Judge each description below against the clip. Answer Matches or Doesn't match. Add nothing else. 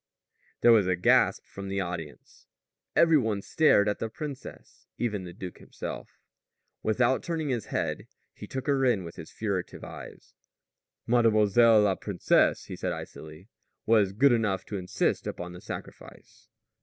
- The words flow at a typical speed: Matches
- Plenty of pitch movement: Doesn't match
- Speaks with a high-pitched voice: Doesn't match